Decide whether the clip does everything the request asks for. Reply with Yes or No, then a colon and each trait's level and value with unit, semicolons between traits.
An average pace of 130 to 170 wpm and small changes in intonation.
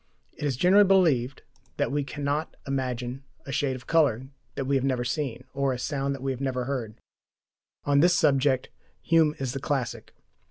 No: average, 185 wpm; narrow, 2.2 semitones